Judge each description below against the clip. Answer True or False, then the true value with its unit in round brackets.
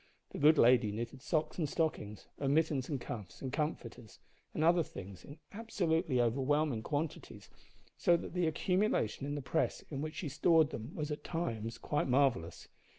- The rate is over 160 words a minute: True (170 wpm)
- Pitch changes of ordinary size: True (4.8 semitones)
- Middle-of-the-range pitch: True (145 Hz)